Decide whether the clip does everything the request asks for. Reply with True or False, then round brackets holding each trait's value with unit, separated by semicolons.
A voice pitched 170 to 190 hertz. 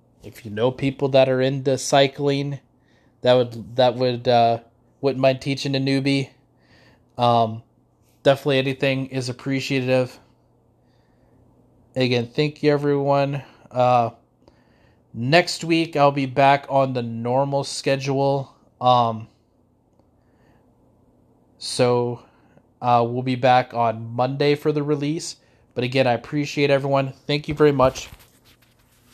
False (135 Hz)